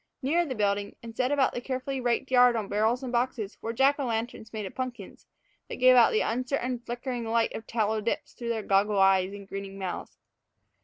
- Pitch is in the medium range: No, high, 235 Hz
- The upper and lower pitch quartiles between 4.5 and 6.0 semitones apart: No, average, 3.4 semitones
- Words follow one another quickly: Yes, fast, 210 wpm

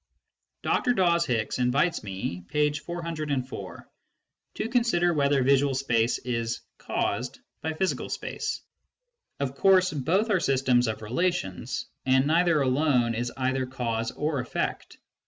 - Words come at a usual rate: No, slow, 130 wpm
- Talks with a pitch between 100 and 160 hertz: Yes, medium, 140 Hz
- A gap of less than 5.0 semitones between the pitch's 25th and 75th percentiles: No, wide, 5.4 semitones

